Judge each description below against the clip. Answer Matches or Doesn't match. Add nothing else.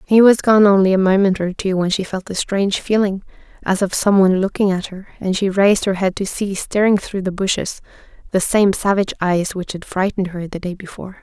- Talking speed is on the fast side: Matches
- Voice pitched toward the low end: Doesn't match